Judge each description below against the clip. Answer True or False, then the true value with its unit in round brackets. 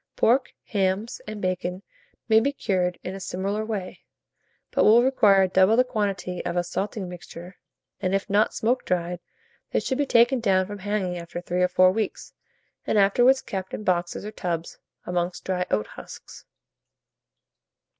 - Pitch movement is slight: False (3.1 semitones)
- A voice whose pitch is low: False (195 Hz)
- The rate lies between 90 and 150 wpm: False (165 wpm)